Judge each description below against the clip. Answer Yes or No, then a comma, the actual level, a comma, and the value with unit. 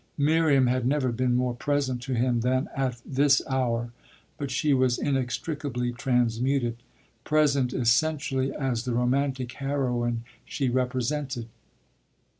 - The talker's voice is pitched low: Yes, low, 130 Hz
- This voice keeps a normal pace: No, slow, 120 wpm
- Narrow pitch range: Yes, narrow, 2.3 semitones